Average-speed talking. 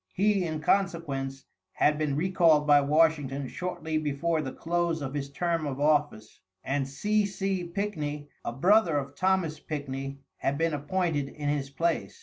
Yes: average, 155 wpm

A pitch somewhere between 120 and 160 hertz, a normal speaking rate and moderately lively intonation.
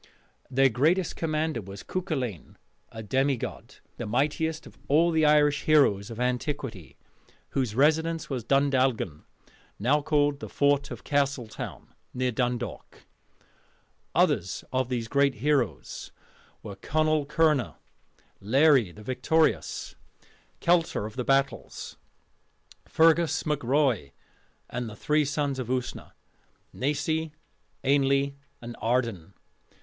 No: medium, 140 Hz; slow, 115 wpm; average, 3.7 semitones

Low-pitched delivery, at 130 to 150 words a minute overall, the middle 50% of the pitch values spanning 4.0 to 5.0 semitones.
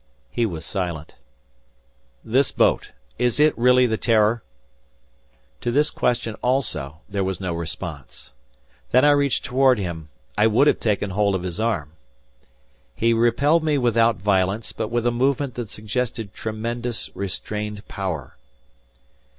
Yes: low, 110 Hz; average, 140 wpm; average, 4.3 semitones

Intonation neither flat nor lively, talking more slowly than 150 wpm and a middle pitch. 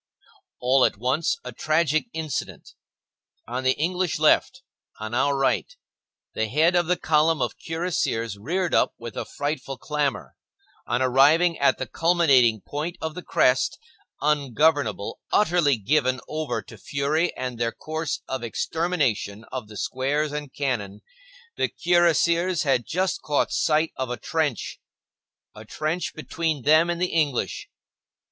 Yes: average, 4.3 semitones; average, 140 wpm; medium, 150 Hz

